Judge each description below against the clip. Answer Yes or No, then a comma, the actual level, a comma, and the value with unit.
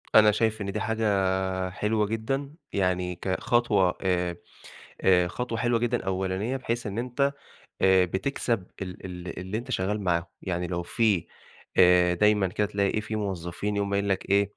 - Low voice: Yes, low, 100 Hz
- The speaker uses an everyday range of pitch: Yes, average, 3.2 semitones